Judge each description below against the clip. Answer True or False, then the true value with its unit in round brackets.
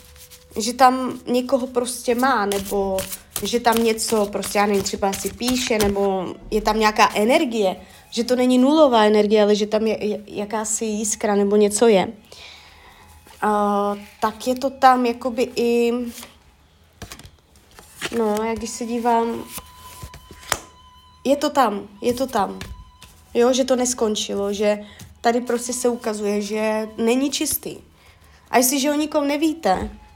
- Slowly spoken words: False (135 wpm)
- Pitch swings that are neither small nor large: True (3.4 semitones)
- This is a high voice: True (220 Hz)